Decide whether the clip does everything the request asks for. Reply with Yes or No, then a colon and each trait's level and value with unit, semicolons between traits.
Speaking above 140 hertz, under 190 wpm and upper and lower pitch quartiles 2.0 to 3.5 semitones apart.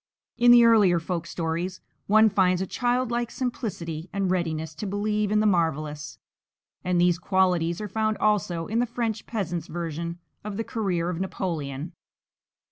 No: medium, 185 Hz; average, 155 wpm; average, 4.2 semitones